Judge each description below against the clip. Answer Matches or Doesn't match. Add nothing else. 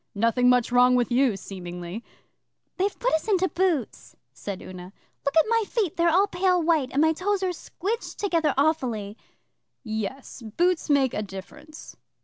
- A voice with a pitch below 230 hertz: Doesn't match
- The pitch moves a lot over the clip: Matches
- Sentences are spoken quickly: Doesn't match